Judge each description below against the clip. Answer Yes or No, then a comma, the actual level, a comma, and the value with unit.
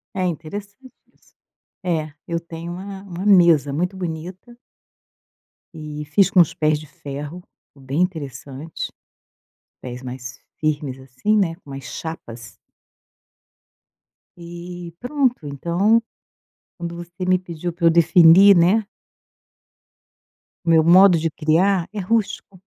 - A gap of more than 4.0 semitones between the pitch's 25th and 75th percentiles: No, average, 3.5 semitones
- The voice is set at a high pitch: No, medium, 170 Hz